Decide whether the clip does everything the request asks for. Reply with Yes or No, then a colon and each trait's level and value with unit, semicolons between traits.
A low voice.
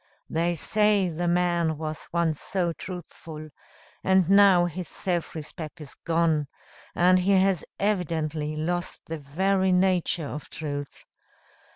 No: medium, 170 Hz